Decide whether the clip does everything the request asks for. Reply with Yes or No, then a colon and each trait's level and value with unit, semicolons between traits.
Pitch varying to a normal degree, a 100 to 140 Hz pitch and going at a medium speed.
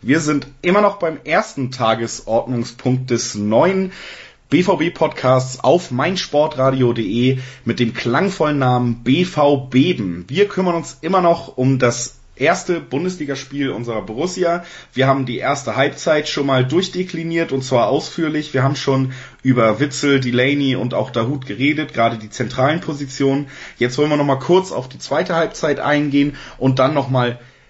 Yes: average, 3.7 semitones; low, 135 Hz; average, 145 wpm